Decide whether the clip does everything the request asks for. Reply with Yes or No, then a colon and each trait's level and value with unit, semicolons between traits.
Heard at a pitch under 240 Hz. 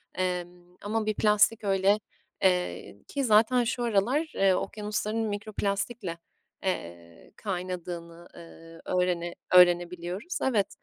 Yes: high, 190 Hz